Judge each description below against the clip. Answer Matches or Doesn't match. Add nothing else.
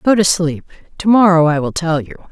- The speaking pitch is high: Doesn't match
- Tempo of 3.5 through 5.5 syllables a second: Doesn't match